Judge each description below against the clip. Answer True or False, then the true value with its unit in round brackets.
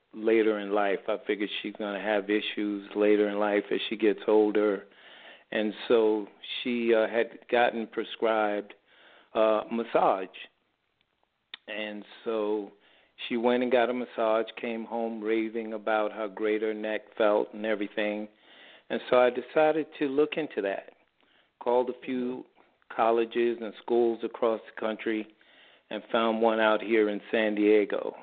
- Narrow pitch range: True (1.6 semitones)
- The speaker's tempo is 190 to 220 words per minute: False (150 wpm)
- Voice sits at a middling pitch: False (110 Hz)